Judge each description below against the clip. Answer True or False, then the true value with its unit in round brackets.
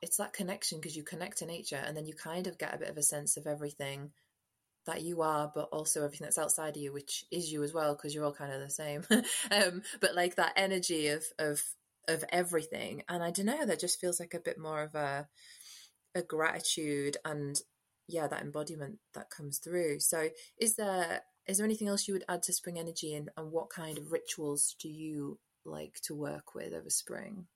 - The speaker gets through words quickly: True (220 wpm)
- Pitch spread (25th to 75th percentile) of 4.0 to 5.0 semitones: False (3.1 semitones)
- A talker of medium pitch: True (160 Hz)